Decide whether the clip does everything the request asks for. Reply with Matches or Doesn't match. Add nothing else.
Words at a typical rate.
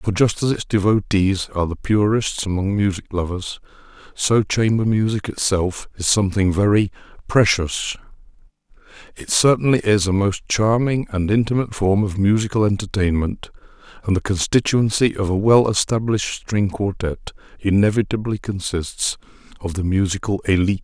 Doesn't match